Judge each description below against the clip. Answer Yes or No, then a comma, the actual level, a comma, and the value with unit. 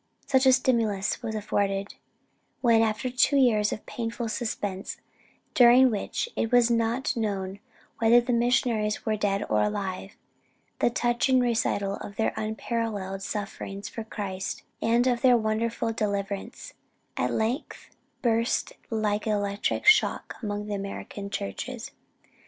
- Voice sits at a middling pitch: No, high, 220 Hz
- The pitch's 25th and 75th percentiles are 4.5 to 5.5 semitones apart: No, average, 2.8 semitones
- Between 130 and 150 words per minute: Yes, slow, 135 wpm